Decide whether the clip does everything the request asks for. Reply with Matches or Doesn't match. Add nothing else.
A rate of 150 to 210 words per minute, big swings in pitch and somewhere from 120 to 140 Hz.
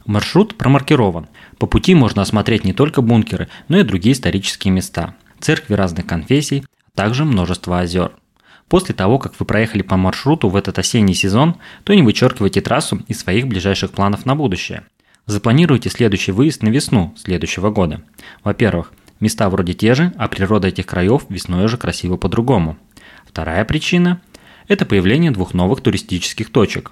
Doesn't match